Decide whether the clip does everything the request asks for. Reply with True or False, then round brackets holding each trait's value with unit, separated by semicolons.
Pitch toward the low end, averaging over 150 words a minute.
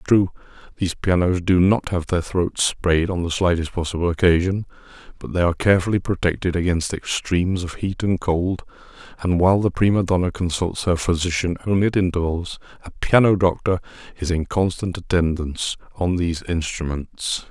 True (90 Hz; 160 wpm)